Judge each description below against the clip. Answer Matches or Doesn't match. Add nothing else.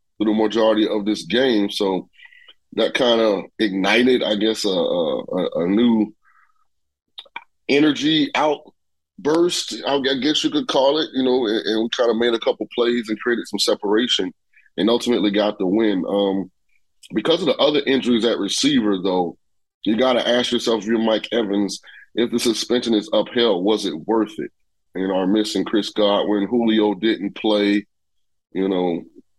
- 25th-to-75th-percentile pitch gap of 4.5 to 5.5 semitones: Doesn't match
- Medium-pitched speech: Doesn't match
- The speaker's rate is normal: Matches